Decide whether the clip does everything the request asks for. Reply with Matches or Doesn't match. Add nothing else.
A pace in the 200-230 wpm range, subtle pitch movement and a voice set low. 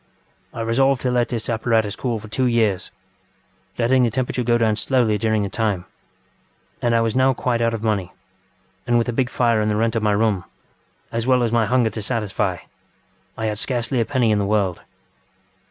Matches